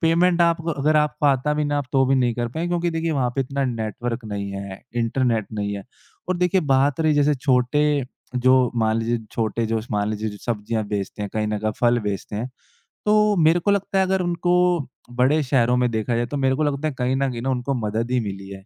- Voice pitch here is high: No, low, 125 Hz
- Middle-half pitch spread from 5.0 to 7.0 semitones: Yes, average, 5.3 semitones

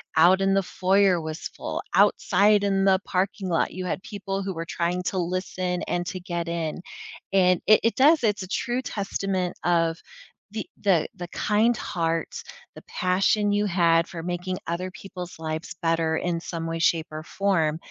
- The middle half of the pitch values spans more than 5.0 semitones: No, average, 2.7 semitones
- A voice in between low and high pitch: Yes, medium, 180 Hz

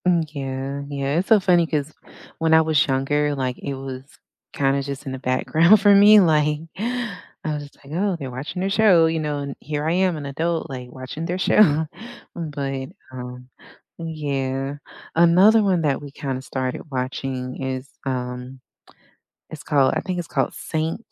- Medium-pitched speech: Yes, medium, 145 Hz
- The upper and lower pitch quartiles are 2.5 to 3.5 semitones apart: No, average, 3.9 semitones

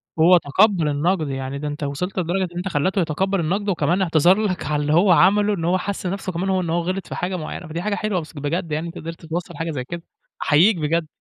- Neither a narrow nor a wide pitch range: Yes, average, 3.3 semitones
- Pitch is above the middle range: No, medium, 175 Hz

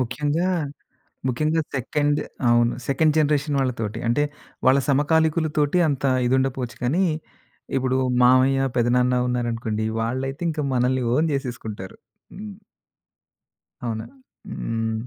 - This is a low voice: Yes, low, 130 Hz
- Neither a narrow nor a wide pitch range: Yes, average, 3.6 semitones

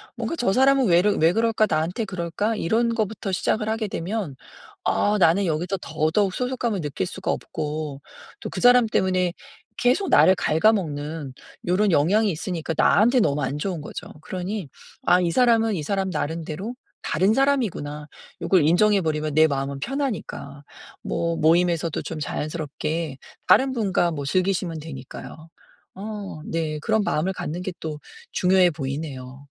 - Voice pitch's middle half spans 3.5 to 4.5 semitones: No, wide, 5.4 semitones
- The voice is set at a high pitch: No, medium, 175 Hz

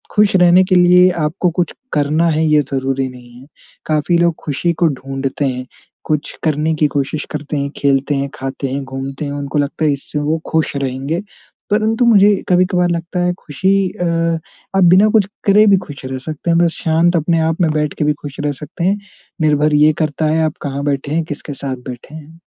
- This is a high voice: No, medium, 155 Hz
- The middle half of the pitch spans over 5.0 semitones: No, average, 3.6 semitones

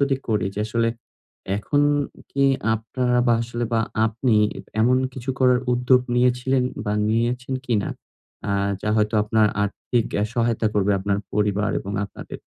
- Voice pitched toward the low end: Yes, low, 115 Hz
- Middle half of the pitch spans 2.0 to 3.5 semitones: Yes, average, 2.9 semitones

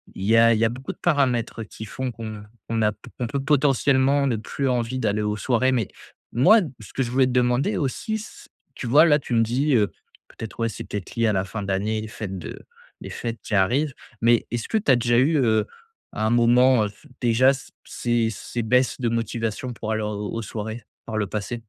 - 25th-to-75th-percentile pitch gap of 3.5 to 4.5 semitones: No, average, 3.0 semitones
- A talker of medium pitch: No, low, 120 Hz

